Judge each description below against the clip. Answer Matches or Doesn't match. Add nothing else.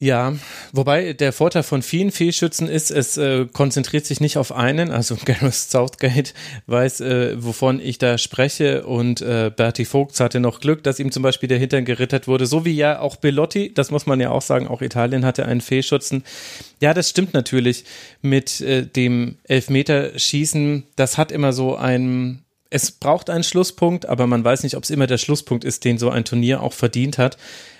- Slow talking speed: Doesn't match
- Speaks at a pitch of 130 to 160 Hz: Matches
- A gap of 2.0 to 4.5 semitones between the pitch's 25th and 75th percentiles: Matches